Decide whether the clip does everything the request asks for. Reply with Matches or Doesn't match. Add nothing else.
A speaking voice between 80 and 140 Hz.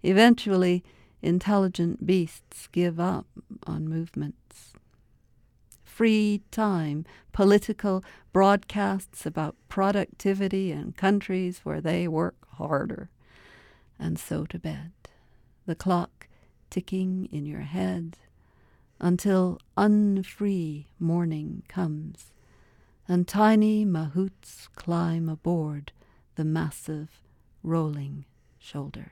Doesn't match